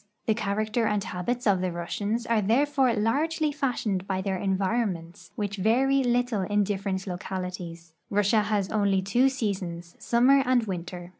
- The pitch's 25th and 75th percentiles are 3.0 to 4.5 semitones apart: Yes, average, 4.1 semitones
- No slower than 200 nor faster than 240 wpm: No, average, 155 wpm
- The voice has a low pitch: No, high, 205 Hz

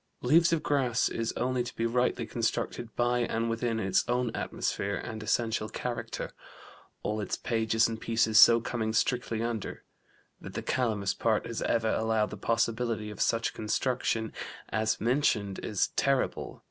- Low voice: Yes, low, 115 Hz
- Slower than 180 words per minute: Yes, average, 155 wpm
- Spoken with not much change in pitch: Yes, narrow, 1.8 semitones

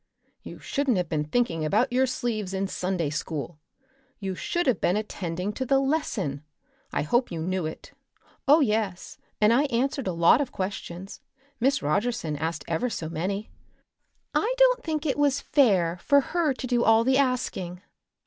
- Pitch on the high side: Yes, high, 215 Hz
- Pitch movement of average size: No, wide, 7.2 semitones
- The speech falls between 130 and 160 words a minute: No, average, 170 wpm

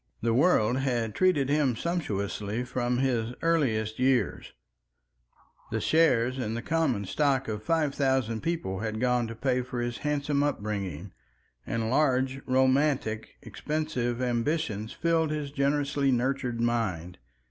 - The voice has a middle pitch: No, low, 125 Hz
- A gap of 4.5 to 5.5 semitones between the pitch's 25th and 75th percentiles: No, average, 4.1 semitones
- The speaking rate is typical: No, slow, 130 wpm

